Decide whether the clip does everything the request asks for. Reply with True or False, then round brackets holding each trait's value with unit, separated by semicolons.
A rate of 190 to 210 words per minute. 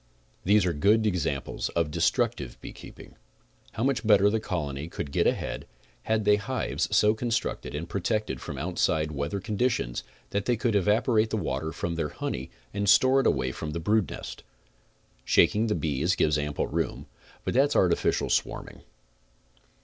False (165 wpm)